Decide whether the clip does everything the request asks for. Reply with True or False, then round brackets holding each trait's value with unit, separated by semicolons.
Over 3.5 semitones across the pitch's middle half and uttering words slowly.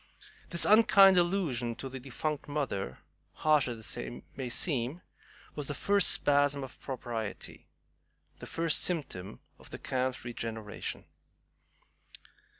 True (5.0 semitones; 120 wpm)